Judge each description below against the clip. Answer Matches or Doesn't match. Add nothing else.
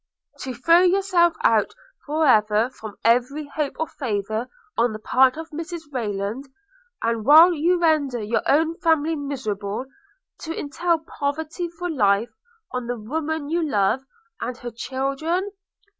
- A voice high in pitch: Matches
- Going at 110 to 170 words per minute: Matches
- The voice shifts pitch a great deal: Matches